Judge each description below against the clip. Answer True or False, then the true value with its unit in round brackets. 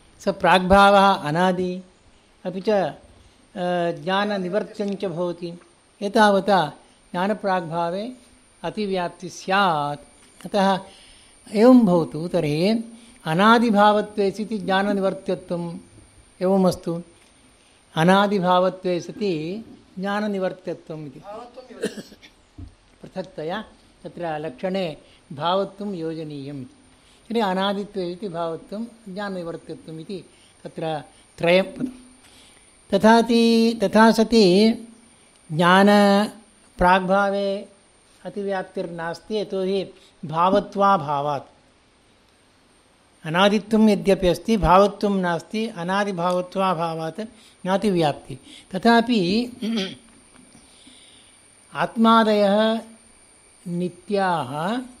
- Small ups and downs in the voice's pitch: False (3.3 semitones)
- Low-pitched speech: False (195 Hz)